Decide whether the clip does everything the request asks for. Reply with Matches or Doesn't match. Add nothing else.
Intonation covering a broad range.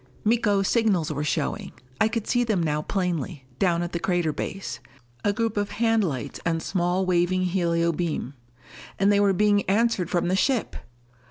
Doesn't match